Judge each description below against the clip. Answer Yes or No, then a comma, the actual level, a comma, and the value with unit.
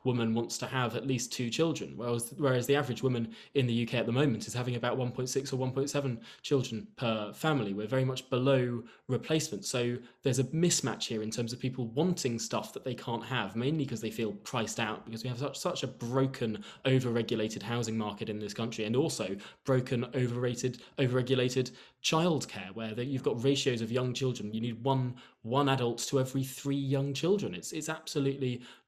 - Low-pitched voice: Yes, low, 125 Hz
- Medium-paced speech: Yes, average, 195 wpm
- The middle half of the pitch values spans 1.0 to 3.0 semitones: Yes, narrow, 2.4 semitones